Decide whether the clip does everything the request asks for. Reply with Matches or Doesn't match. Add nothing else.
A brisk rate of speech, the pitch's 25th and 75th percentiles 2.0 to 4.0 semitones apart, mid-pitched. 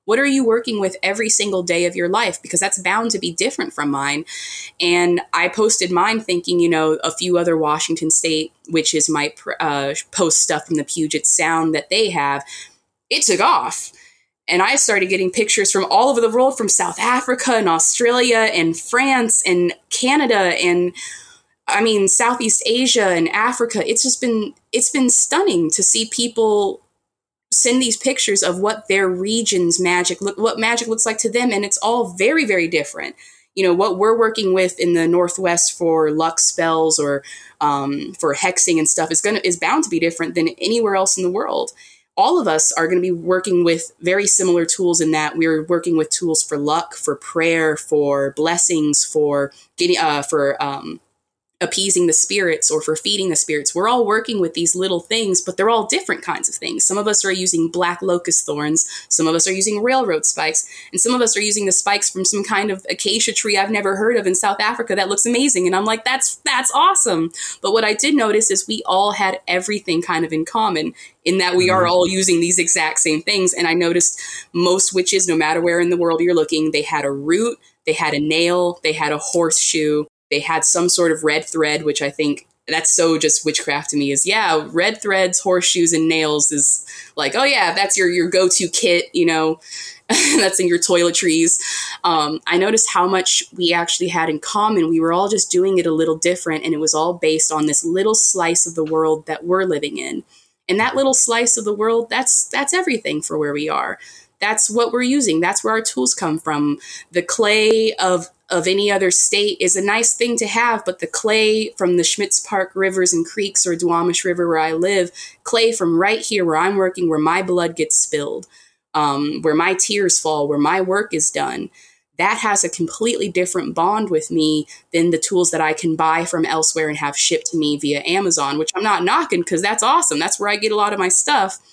Doesn't match